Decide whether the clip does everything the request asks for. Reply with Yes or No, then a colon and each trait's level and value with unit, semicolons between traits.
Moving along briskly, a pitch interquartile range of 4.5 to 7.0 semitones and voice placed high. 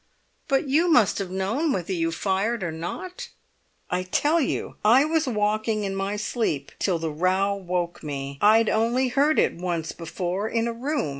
No: average, 175 wpm; wide, 5.5 semitones; high, 205 Hz